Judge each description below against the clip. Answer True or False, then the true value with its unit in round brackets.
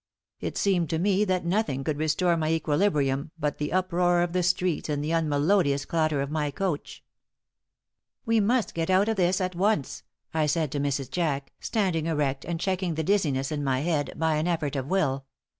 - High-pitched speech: False (160 Hz)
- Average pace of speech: True (190 wpm)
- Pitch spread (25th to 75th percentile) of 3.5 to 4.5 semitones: True (4.0 semitones)